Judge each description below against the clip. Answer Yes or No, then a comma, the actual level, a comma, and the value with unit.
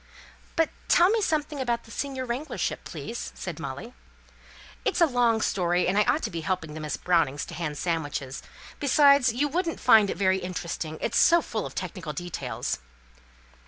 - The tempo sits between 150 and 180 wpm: Yes, average, 175 wpm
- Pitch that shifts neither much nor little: No, wide, 8.7 semitones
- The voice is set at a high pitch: Yes, high, 205 Hz